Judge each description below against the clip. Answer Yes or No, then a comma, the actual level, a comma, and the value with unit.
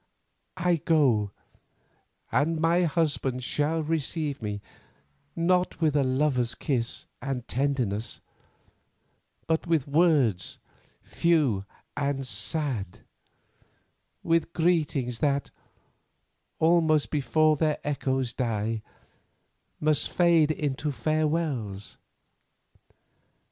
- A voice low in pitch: No, medium, 145 Hz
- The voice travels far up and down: No, average, 4.3 semitones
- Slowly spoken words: Yes, slow, 85 wpm